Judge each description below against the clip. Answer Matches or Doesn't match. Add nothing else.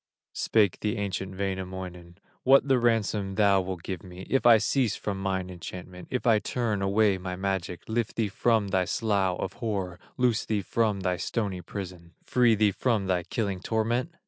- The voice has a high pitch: Doesn't match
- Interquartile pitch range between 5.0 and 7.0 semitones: Doesn't match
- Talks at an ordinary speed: Matches